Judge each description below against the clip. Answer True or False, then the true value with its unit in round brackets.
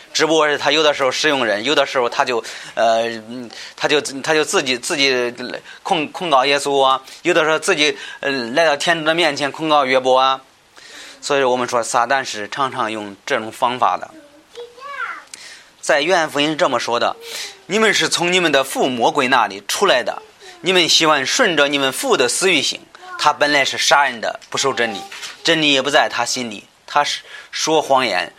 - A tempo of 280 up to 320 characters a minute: False (270 characters per minute)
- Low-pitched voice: False (145 Hz)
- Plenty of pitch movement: False (4.2 semitones)